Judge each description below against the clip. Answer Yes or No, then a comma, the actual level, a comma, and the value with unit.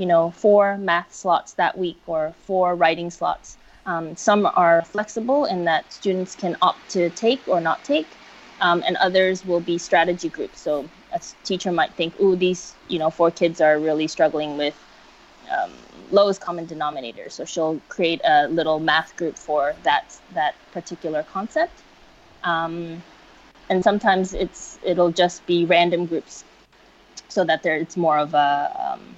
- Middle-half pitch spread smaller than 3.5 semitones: Yes, average, 2.9 semitones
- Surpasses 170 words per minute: No, average, 165 wpm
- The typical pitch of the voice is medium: Yes, medium, 175 Hz